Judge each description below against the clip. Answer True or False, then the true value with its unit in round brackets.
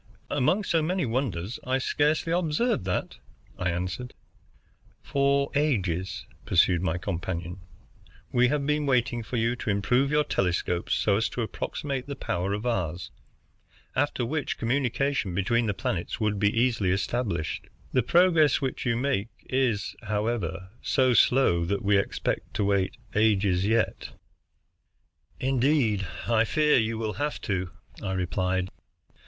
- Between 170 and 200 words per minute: False (140 wpm)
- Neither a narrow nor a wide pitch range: False (6.2 semitones)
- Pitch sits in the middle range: False (115 Hz)